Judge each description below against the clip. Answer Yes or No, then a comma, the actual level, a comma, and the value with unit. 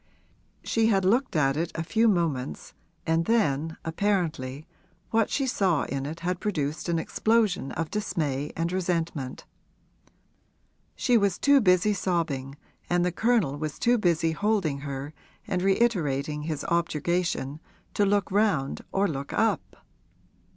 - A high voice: No, medium, 170 Hz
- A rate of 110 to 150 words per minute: Yes, slow, 135 wpm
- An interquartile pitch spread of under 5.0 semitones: No, average, 5.3 semitones